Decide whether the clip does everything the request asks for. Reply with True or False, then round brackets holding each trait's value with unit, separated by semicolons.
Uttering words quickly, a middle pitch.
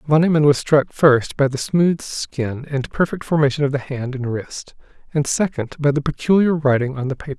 True (210 wpm; 145 Hz)